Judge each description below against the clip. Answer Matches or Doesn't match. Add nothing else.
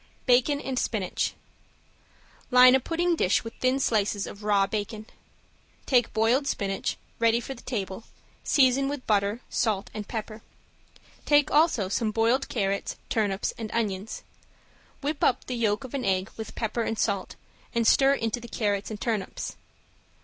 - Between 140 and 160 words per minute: Matches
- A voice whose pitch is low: Doesn't match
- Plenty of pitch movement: Doesn't match